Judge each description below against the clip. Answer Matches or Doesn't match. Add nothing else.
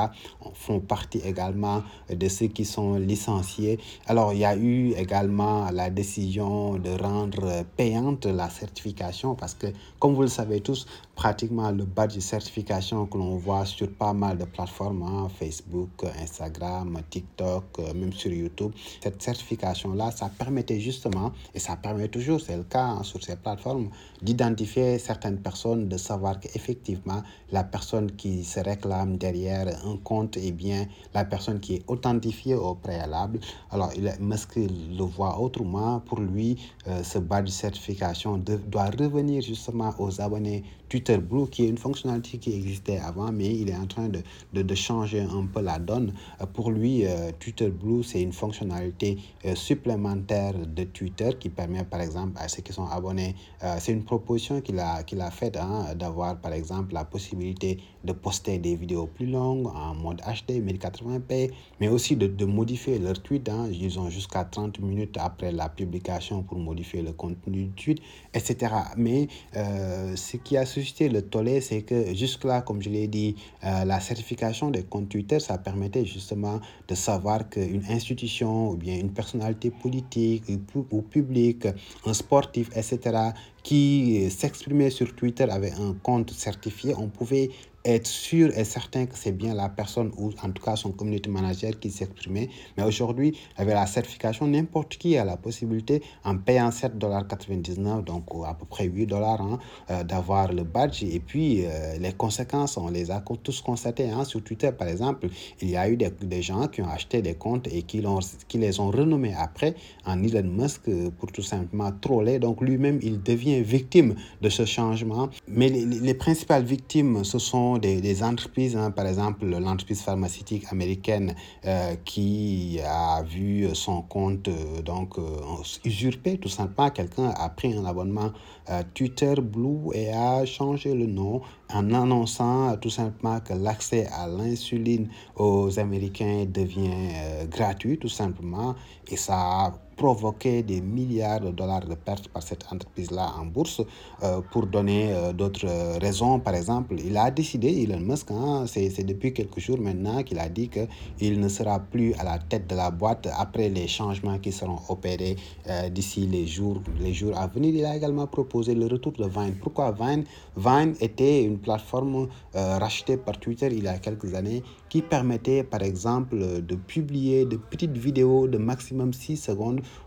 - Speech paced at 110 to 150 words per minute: Doesn't match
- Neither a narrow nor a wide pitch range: Matches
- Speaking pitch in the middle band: Doesn't match